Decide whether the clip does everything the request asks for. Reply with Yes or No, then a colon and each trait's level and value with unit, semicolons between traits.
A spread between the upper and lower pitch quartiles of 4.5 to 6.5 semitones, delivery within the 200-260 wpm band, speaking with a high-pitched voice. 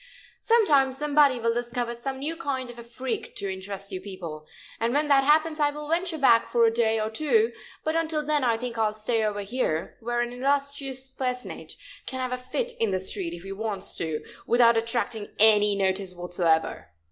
Yes: average, 5.1 semitones; fast, 205 wpm; high, 240 Hz